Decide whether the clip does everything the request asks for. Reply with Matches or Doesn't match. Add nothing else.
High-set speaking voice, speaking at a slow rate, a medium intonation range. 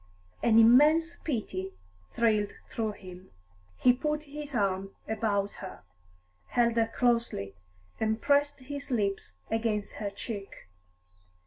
Matches